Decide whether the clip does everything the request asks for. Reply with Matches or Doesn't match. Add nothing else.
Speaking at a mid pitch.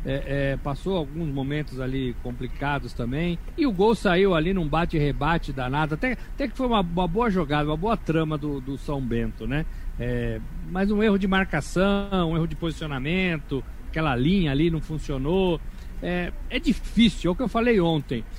Matches